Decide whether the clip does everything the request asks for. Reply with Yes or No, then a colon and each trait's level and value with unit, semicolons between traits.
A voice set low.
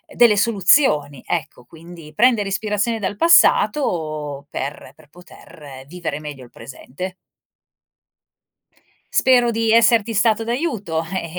No: medium, 185 Hz